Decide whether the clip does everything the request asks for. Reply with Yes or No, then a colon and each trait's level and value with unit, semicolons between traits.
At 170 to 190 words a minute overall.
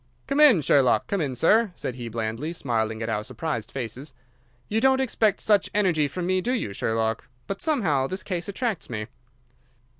Yes: average, 180 wpm